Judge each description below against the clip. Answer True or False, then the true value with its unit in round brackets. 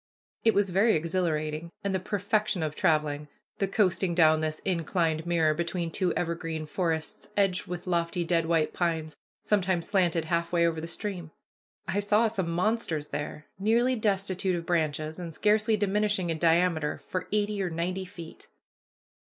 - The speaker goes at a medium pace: True (160 wpm)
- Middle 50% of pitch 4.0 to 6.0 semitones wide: False (3.4 semitones)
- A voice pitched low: False (175 Hz)